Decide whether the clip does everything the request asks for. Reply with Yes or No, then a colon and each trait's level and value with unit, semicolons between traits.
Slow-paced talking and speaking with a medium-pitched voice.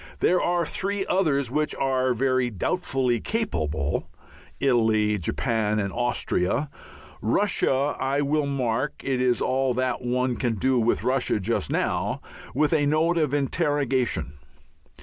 No: slow, 130 wpm; low, 130 Hz